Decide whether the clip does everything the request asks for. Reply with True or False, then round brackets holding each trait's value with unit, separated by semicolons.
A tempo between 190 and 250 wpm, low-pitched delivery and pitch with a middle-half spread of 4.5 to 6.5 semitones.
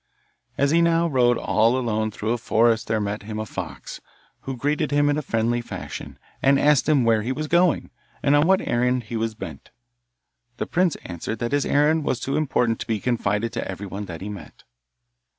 True (205 wpm; 120 Hz; 4.9 semitones)